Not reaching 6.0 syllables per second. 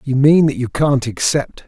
Yes: 5.0 syllables/s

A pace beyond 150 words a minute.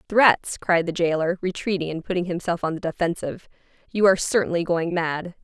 Yes: average, 175 wpm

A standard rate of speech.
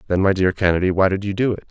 No: fast, 315 wpm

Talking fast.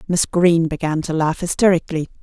No: average, 160 wpm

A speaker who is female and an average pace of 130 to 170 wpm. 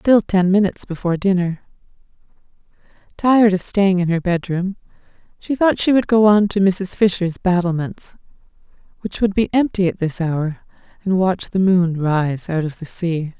Yes: female; average, 165 wpm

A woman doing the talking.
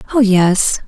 Yes: female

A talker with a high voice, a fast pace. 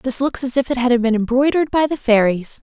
Yes: very high, 250 Hz; fast, 240 wpm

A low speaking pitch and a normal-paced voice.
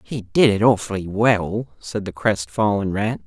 Yes: low, 105 Hz; average, 165 wpm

